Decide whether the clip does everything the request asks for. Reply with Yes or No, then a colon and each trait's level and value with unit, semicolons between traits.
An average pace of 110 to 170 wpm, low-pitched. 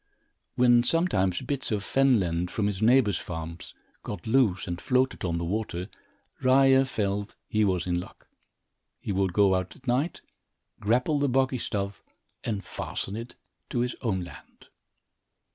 Yes: average, 155 wpm; low, 105 Hz